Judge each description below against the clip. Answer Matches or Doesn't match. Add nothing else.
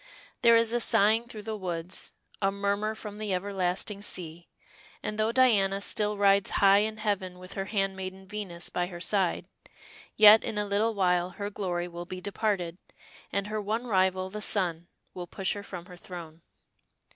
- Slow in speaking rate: Doesn't match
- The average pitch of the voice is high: Matches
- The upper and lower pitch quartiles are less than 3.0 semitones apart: Matches